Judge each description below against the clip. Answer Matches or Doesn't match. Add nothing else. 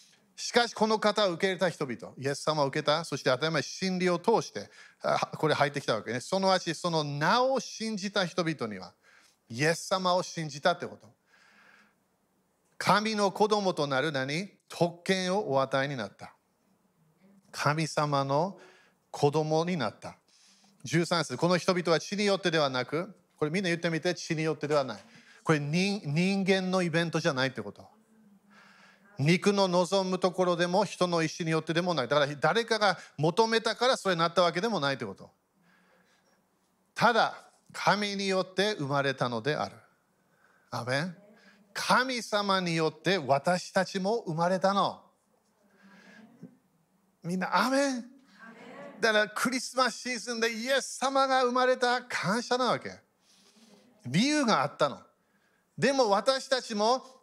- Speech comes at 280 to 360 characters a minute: Matches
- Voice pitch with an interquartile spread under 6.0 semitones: Matches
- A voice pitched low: Doesn't match